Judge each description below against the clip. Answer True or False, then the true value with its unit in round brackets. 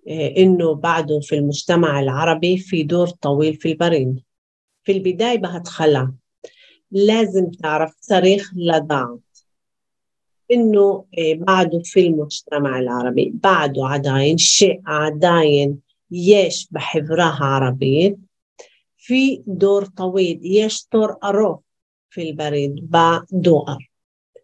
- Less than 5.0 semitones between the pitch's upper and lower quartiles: True (4.6 semitones)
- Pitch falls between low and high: True (165 Hz)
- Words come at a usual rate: False (95 wpm)